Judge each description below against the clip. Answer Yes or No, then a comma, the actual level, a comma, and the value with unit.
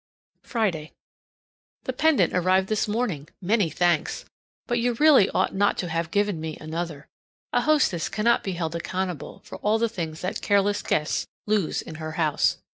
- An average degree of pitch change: Yes, average, 4.9 semitones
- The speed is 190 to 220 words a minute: No, average, 165 wpm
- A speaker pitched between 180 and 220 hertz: Yes, medium, 185 Hz